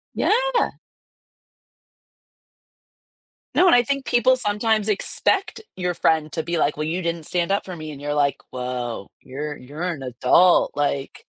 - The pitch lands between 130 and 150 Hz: No, medium, 170 Hz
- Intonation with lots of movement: Yes, wide, 6.4 semitones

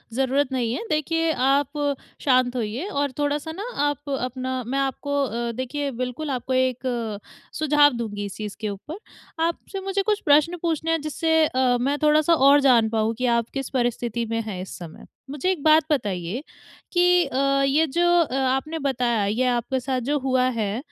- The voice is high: Yes, very high, 265 Hz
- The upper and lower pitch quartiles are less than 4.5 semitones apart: Yes, average, 3.8 semitones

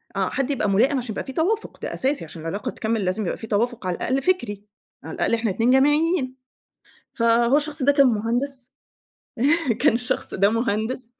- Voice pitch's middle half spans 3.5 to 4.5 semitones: Yes, average, 4.1 semitones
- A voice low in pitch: No, high, 240 Hz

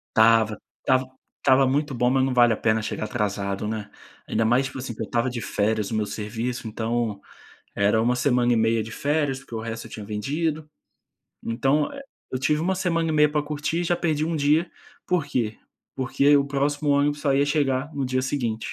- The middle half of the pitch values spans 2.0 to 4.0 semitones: No, average, 4.6 semitones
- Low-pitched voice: Yes, low, 130 Hz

